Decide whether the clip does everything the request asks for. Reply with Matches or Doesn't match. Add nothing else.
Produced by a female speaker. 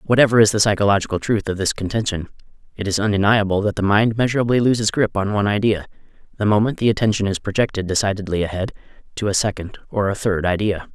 Doesn't match